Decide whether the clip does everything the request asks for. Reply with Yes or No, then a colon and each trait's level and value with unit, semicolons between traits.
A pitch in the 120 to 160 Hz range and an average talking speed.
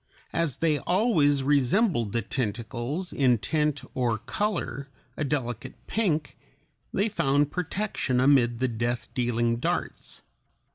No: low, 135 Hz; slow, 115 wpm